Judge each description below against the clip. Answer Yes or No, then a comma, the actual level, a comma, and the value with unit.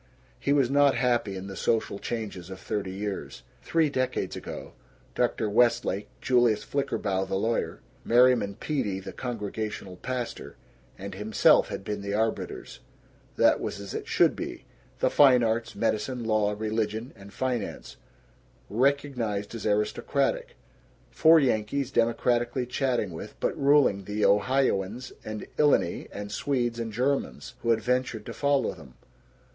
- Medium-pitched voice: No, low, 115 Hz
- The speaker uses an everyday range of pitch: Yes, average, 3.8 semitones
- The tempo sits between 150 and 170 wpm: No, average, 140 wpm